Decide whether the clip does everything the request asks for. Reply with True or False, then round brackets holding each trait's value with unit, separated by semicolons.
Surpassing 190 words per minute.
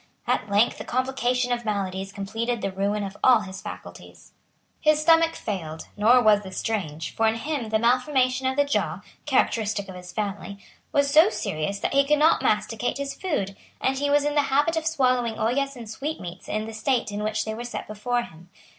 True (200 wpm)